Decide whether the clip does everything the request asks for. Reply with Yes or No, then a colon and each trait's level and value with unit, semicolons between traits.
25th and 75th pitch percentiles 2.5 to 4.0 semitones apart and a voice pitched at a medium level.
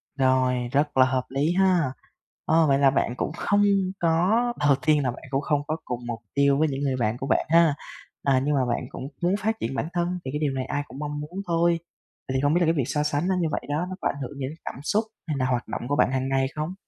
Yes: average, 3.7 semitones; medium, 145 Hz